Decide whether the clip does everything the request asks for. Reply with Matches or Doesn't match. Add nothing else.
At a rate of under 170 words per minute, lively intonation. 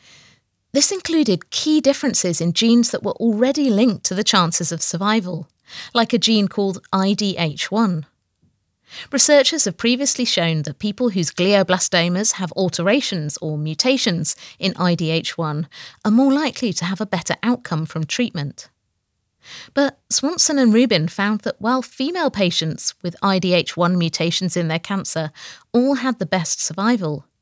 Matches